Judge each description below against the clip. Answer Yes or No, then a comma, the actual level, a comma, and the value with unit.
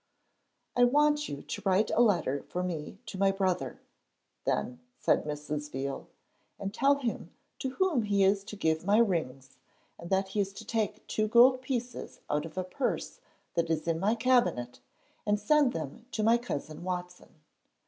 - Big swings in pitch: Yes, wide, 6.4 semitones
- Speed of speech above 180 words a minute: No, average, 175 wpm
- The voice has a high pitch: Yes, high, 195 Hz